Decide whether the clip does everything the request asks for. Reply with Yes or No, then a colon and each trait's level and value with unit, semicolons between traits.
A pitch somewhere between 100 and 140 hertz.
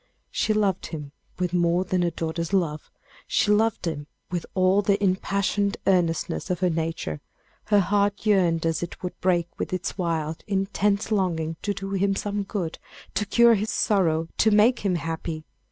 No: medium, 185 Hz